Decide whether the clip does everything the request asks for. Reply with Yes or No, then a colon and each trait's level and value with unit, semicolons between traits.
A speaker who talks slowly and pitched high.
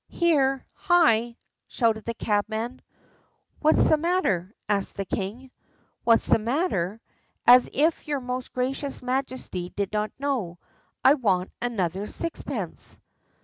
Yes: slow, 120 wpm; high, 240 Hz